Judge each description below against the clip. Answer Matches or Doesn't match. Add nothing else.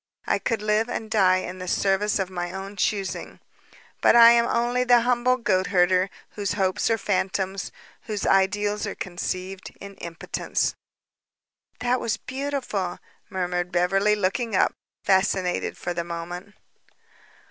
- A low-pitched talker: Doesn't match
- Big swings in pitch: Doesn't match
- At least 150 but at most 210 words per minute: Doesn't match